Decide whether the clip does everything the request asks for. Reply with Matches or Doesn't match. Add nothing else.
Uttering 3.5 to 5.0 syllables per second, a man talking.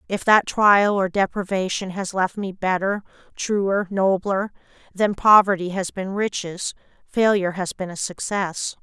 Doesn't match